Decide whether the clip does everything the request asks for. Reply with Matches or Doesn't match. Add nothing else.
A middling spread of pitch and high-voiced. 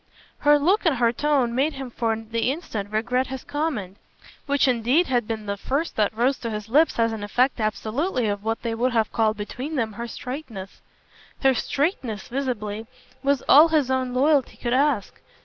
Matches